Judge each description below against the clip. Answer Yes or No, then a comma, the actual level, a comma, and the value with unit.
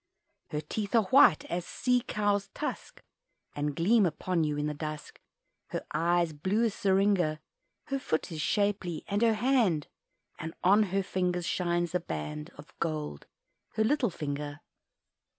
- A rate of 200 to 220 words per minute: No, average, 150 wpm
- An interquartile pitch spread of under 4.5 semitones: No, average, 5.2 semitones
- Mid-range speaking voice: Yes, medium, 180 Hz